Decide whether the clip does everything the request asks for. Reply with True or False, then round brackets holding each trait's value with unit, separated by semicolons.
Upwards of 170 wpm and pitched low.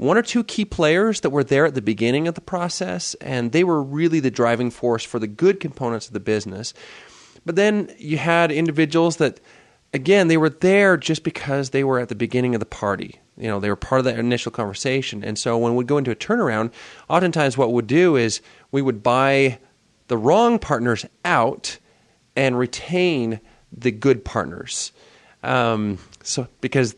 True (190 wpm; 130 Hz)